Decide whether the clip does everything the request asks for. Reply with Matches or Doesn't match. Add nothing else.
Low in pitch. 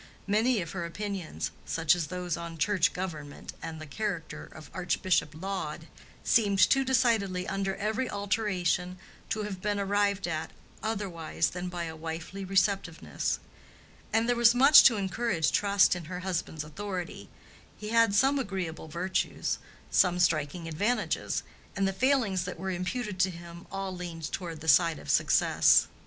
Doesn't match